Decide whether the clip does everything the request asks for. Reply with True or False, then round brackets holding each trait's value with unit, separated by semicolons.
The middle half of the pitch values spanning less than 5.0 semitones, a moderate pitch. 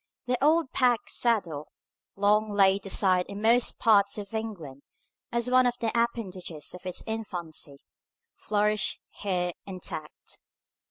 False (4.2 semitones; 205 Hz)